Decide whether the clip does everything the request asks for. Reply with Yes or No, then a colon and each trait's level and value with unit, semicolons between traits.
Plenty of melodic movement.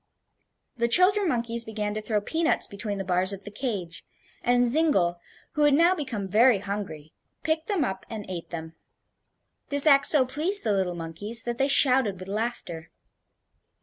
Yes: wide, 6.3 semitones